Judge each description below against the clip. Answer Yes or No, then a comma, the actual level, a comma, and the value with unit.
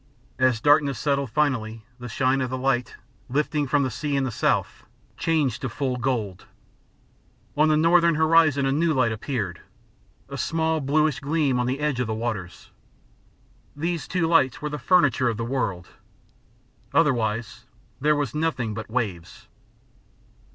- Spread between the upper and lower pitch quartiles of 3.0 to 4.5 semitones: Yes, average, 4.0 semitones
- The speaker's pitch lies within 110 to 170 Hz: Yes, low, 135 Hz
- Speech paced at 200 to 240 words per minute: No, average, 155 wpm